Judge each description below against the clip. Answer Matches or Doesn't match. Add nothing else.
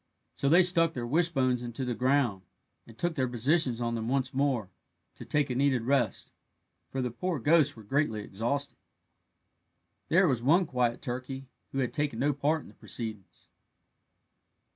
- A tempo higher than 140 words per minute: Matches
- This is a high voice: Doesn't match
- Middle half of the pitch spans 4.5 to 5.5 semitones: Doesn't match